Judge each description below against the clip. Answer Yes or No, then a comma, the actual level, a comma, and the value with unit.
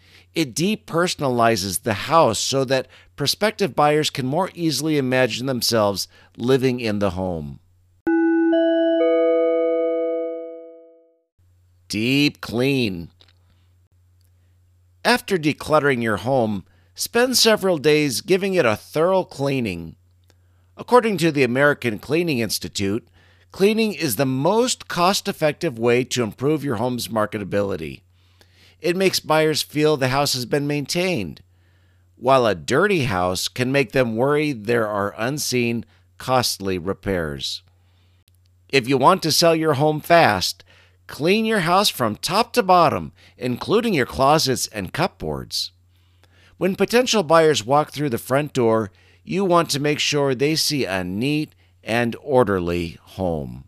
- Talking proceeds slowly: Yes, slow, 125 wpm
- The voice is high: No, low, 130 Hz